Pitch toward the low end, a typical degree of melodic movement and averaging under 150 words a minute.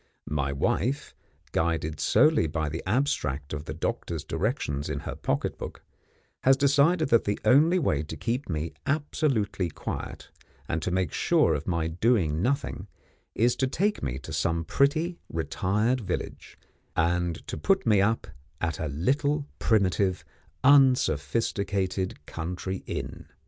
No: very low, 95 Hz; wide, 8.8 semitones; average, 140 wpm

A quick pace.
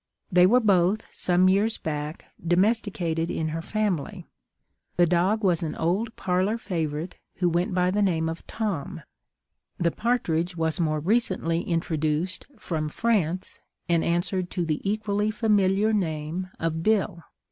No: average, 140 wpm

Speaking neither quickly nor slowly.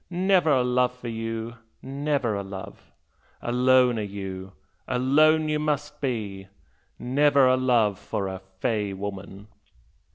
No: slow, 130 wpm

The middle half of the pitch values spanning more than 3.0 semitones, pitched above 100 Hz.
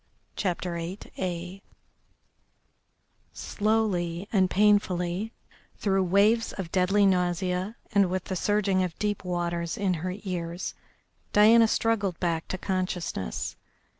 No: narrow, 2.6 semitones; medium, 185 Hz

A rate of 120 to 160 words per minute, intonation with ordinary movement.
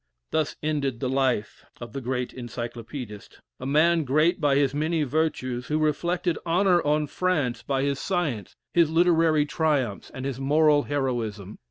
Yes: average, 155 wpm; average, 3.9 semitones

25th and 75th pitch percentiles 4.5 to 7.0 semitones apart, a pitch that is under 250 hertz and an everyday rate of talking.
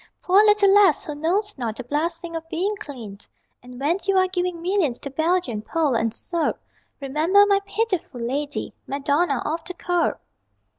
No: average, 5.1 semitones; very high, 330 Hz; average, 165 wpm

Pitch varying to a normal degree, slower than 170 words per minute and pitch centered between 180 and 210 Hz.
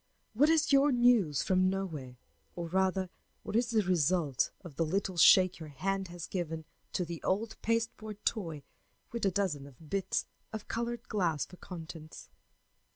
Yes: average, 4.9 semitones; average, 155 wpm; medium, 185 Hz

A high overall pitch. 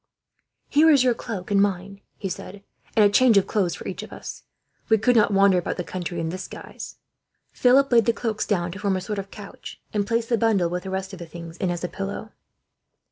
Yes: high, 200 Hz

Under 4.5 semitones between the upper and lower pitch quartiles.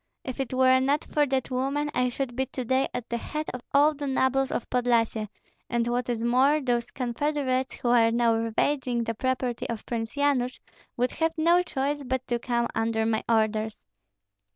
Yes: narrow, 2.4 semitones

